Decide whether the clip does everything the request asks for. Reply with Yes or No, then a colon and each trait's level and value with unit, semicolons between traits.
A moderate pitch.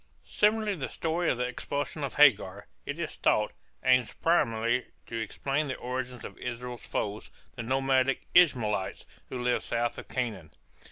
No: low, 125 Hz